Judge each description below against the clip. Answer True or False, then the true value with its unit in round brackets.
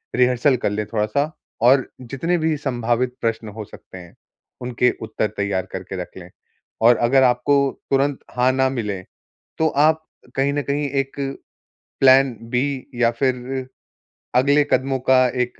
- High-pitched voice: False (130 Hz)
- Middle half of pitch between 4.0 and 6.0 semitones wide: False (2.8 semitones)